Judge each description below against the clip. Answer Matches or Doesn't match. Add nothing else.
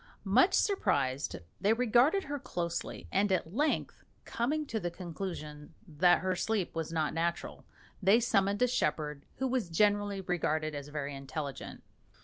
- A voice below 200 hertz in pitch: Matches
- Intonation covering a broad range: Matches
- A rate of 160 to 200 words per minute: Doesn't match